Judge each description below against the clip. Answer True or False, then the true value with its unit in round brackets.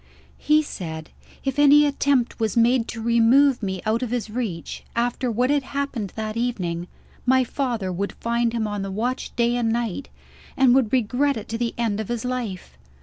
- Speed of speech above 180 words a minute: True (190 wpm)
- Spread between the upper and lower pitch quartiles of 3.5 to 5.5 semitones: False (2.9 semitones)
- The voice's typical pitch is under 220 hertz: False (235 Hz)